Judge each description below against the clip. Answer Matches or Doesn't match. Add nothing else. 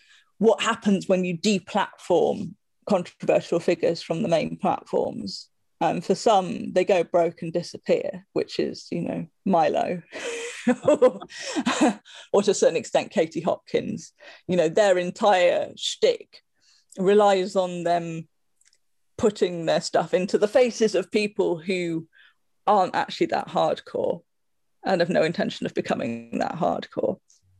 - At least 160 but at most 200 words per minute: Doesn't match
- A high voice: Matches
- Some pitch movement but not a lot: Doesn't match